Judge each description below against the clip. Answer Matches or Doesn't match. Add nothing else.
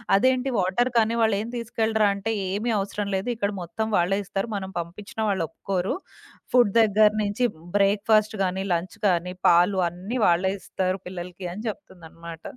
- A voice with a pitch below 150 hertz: Doesn't match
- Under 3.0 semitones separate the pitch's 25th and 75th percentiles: Doesn't match